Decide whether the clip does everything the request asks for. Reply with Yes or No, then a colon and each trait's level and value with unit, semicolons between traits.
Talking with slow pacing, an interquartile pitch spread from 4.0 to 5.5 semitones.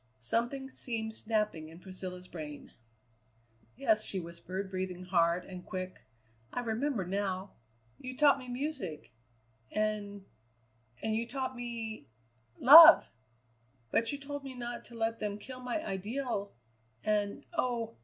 Yes: slow, 130 wpm; average, 5.0 semitones